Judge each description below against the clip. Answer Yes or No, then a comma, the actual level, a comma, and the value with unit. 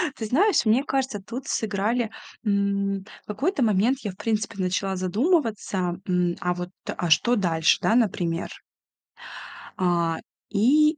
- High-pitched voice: Yes, high, 205 Hz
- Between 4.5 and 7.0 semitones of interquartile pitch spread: Yes, average, 5.0 semitones